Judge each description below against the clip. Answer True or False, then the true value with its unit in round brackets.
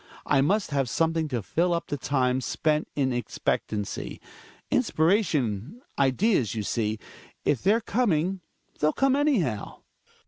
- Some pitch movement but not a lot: False (7.3 semitones)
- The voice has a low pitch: False (150 Hz)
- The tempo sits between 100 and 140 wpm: True (135 wpm)